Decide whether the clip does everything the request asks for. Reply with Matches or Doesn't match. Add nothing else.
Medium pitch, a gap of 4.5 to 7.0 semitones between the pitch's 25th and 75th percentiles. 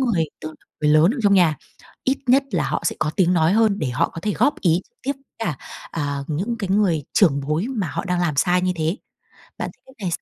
Matches